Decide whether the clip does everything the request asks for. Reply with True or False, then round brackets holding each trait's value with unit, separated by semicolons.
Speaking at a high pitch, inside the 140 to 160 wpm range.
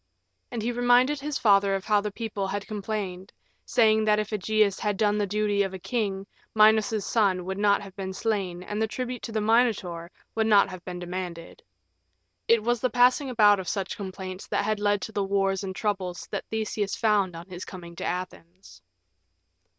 False (205 Hz; 195 wpm)